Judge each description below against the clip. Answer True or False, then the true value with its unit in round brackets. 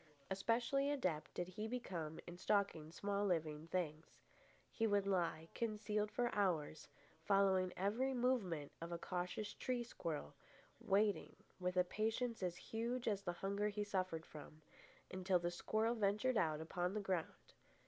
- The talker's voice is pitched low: False (195 Hz)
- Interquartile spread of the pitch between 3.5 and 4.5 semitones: True (3.9 semitones)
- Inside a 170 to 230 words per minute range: False (150 wpm)